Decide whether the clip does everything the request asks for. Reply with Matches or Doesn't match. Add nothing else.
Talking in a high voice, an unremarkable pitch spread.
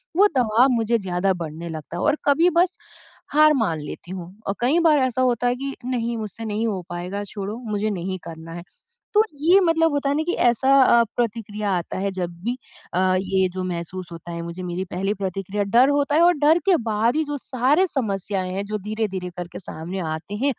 Doesn't match